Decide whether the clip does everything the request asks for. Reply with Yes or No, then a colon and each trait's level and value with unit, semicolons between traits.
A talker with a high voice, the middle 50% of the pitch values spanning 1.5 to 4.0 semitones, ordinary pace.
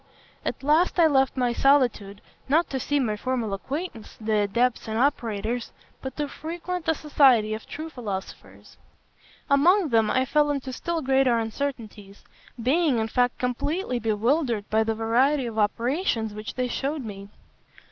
No: very high, 250 Hz; average, 4.6 semitones; average, 155 wpm